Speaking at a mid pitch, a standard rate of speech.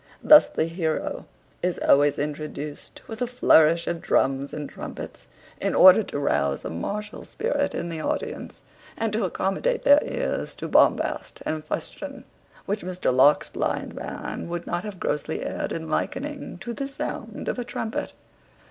Yes: medium, 175 Hz; average, 160 wpm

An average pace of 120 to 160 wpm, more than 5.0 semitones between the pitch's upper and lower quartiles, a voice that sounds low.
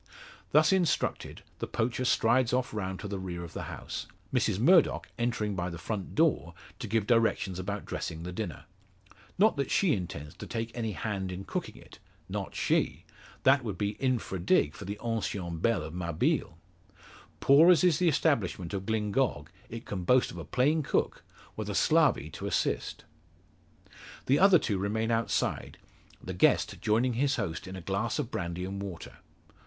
No: average, 175 wpm; wide, 5.4 semitones; low, 105 Hz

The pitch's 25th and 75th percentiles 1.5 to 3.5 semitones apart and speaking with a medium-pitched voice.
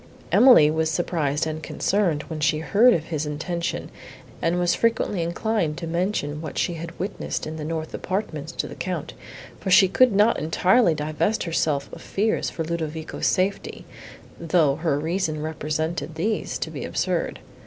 Yes: average, 3.0 semitones; medium, 165 Hz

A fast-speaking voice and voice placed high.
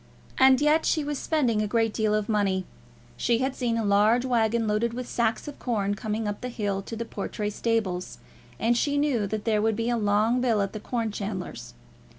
Yes: fast, 210 wpm; high, 225 Hz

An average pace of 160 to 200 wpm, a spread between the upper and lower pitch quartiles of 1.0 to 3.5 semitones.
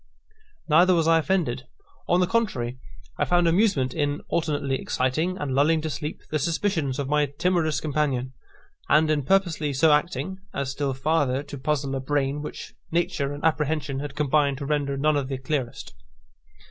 Yes: average, 170 wpm; average, 3.0 semitones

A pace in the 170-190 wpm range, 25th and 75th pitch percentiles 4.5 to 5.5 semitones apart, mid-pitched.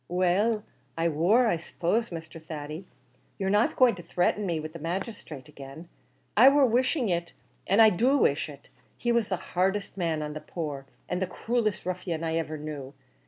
Yes: average, 185 wpm; average, 5.2 semitones; medium, 175 Hz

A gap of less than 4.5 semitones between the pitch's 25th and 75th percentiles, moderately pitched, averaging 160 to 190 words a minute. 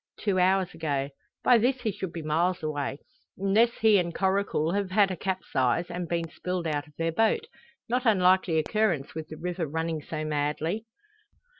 Yes: average, 3.9 semitones; medium, 175 Hz; average, 175 wpm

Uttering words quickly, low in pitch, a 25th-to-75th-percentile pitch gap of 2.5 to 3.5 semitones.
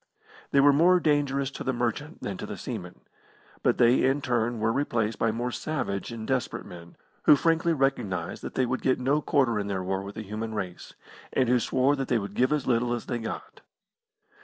No: fast, 210 wpm; low, 125 Hz; average, 4.0 semitones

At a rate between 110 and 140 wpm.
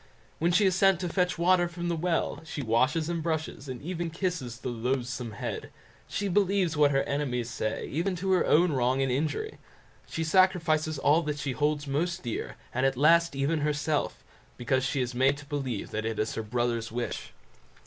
No: average, 195 wpm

